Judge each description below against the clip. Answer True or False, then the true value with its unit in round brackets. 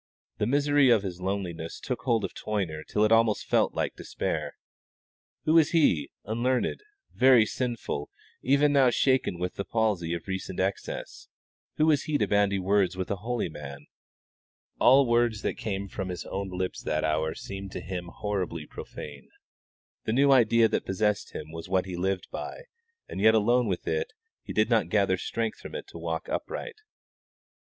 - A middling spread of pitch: True (5.0 semitones)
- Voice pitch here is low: True (105 Hz)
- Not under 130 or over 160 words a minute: False (175 wpm)